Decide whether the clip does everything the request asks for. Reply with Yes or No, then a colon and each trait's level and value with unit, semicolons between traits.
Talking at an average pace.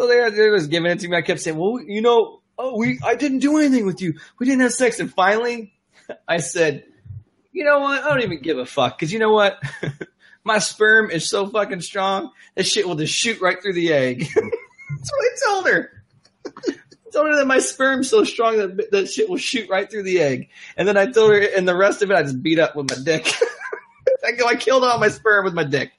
No: fast, 240 wpm